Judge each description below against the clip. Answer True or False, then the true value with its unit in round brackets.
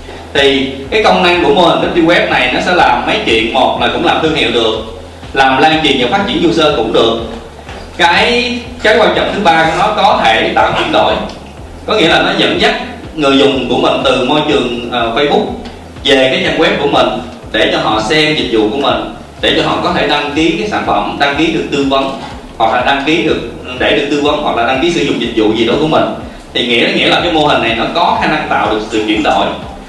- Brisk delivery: True (255 wpm)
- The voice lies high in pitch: False (135 Hz)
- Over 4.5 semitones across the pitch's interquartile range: True (5.2 semitones)